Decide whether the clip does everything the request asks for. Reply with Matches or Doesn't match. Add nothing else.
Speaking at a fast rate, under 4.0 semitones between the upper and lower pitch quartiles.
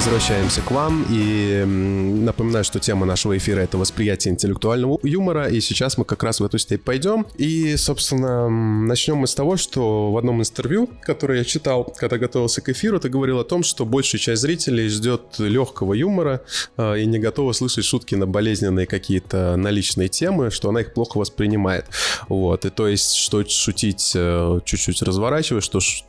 Doesn't match